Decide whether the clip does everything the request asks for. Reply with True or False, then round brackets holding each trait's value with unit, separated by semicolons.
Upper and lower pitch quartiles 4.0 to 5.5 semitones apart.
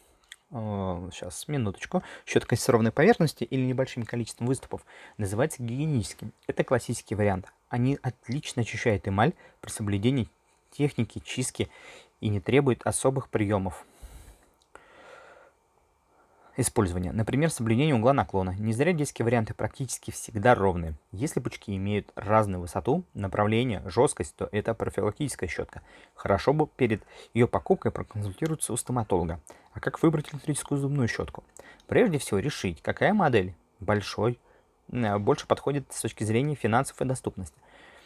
True (4.7 semitones)